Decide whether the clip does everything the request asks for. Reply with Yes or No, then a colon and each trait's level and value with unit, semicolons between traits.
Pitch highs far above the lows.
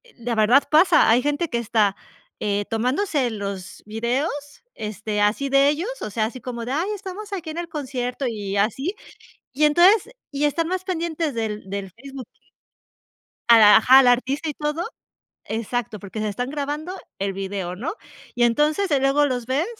Yes: wide, 5.7 semitones